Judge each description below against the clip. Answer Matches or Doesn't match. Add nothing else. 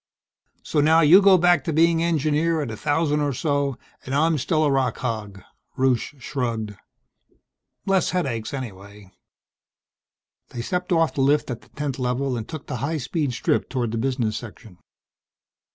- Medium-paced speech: Matches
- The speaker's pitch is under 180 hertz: Matches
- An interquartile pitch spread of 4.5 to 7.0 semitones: Matches